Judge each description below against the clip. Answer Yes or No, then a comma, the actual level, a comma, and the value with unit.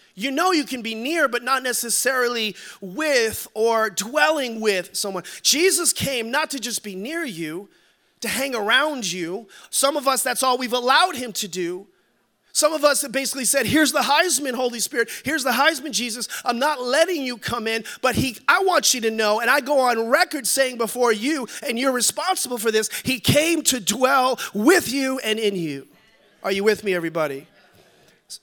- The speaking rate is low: No, average, 190 wpm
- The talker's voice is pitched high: Yes, very high, 250 Hz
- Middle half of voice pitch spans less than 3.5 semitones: No, average, 4.7 semitones